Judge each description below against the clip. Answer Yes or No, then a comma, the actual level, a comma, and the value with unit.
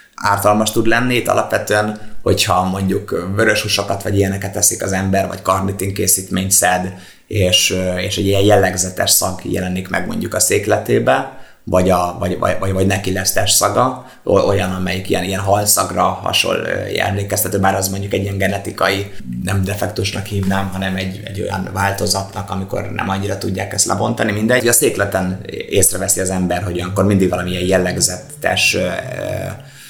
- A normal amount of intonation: No, narrow, 1.4 semitones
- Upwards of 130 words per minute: Yes, fast, 155 wpm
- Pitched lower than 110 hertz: Yes, very low, 95 Hz